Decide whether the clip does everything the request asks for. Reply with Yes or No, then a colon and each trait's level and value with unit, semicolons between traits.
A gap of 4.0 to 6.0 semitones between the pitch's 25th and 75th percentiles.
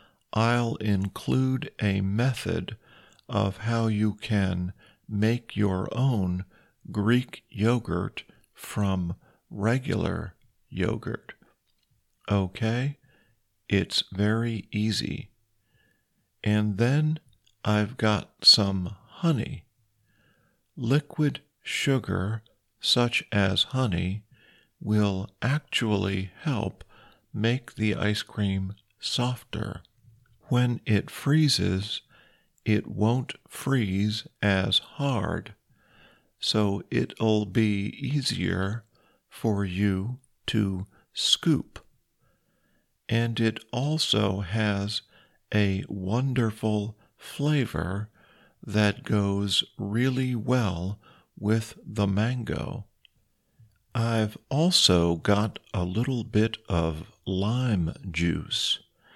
No: average, 3.2 semitones